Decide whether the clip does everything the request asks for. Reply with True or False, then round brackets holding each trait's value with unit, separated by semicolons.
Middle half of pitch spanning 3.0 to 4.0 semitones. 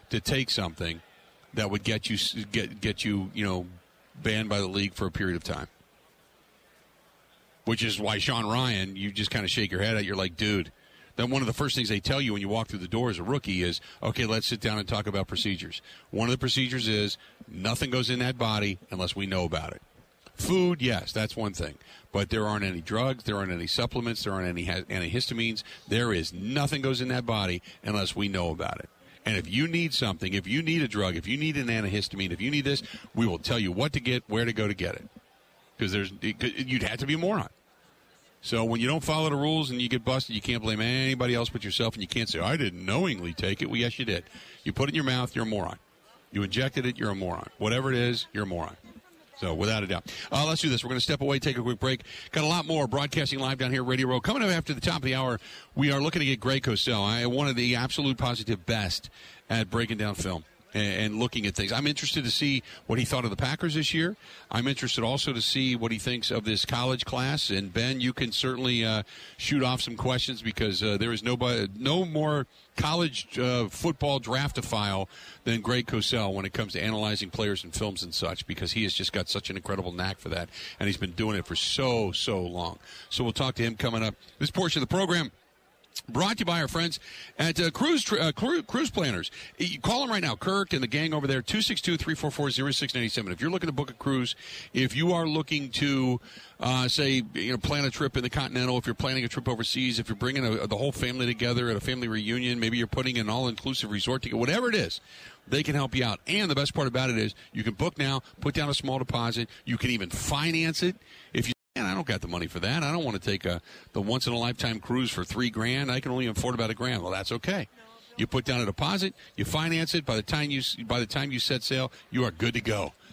False (4.5 semitones)